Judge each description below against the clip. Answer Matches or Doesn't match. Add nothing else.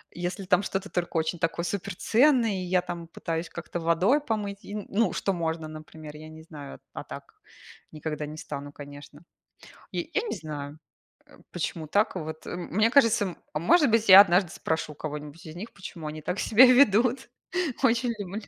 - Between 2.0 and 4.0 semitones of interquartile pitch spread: Doesn't match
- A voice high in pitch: Doesn't match